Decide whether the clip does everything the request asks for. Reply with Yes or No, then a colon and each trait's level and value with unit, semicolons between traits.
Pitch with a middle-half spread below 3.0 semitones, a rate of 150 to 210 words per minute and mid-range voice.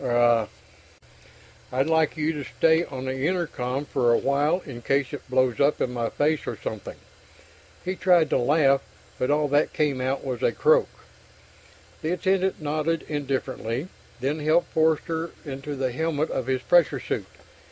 No: average, 3.6 semitones; average, 165 wpm; medium, 145 Hz